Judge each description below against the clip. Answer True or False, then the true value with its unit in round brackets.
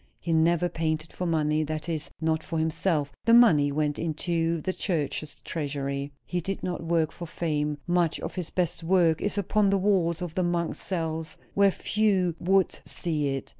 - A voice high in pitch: False (165 Hz)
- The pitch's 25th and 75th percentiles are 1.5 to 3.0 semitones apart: True (2.5 semitones)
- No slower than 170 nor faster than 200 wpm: True (180 wpm)